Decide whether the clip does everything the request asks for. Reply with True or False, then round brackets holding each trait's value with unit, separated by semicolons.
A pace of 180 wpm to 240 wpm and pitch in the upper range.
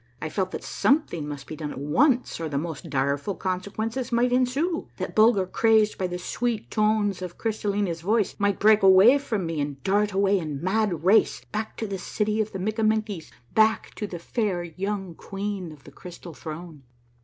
True (190 wpm; 195 Hz)